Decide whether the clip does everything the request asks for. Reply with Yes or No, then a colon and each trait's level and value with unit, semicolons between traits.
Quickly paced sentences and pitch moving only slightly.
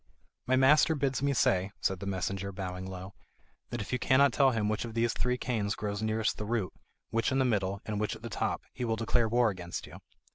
No: fast, 230 wpm; average, 4.1 semitones